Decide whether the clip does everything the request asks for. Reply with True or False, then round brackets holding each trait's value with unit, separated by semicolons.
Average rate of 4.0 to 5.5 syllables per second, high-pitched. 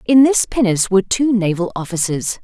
False (5.7 syllables/s; 205 Hz)